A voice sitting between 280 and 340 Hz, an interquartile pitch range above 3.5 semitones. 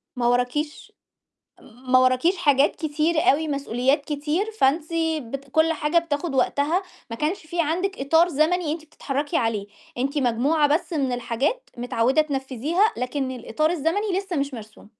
Yes: very high, 290 Hz; average, 4.0 semitones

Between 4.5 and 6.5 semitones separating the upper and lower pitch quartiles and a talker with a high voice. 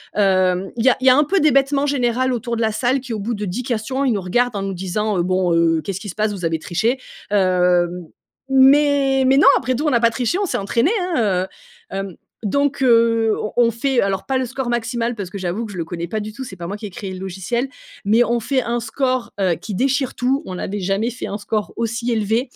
Yes: average, 4.9 semitones; high, 230 Hz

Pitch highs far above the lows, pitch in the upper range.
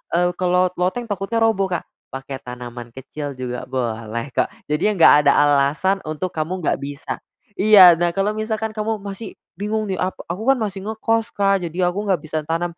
No: wide, 6.2 semitones; medium, 180 Hz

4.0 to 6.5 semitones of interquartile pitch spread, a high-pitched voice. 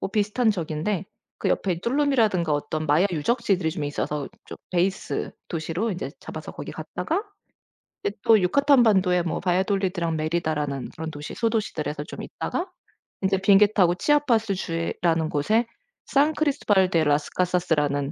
No: average, 5.3 semitones; medium, 180 Hz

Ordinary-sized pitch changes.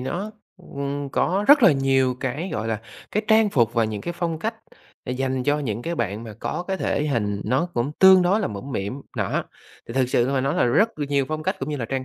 No: wide, 6.1 semitones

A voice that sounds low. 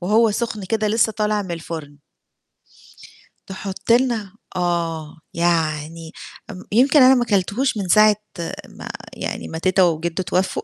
No: high, 190 Hz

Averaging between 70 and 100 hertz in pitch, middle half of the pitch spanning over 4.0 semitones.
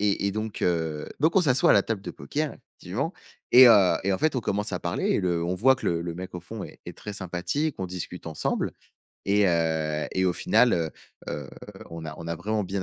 Yes: very low, 95 Hz; average, 4.5 semitones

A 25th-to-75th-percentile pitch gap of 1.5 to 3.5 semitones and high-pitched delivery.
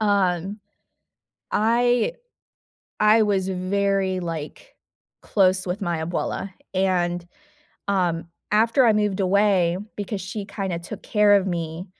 Yes: average, 2.7 semitones; high, 195 Hz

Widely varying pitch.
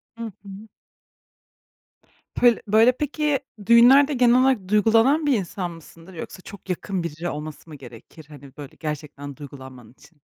Yes: wide, 7.8 semitones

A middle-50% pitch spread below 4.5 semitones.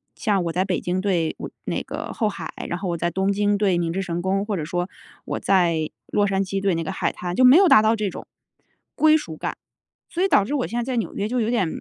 Yes: average, 3.3 semitones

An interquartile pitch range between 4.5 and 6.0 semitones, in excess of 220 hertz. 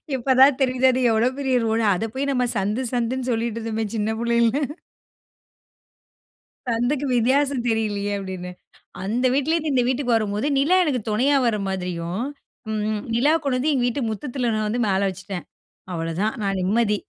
No: average, 3.8 semitones; high, 235 Hz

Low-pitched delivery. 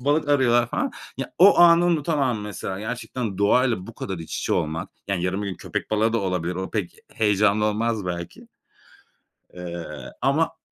Yes: low, 105 Hz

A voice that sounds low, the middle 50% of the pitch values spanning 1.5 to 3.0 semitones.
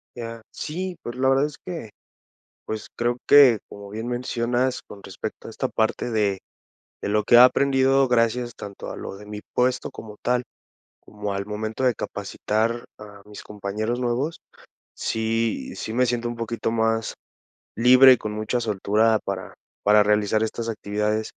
Yes: low, 115 Hz; average, 2.7 semitones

